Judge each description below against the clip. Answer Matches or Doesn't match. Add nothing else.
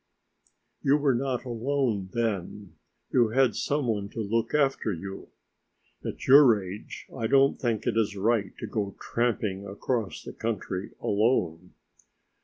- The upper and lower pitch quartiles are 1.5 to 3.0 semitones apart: Doesn't match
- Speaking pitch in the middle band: Doesn't match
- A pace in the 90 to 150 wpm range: Matches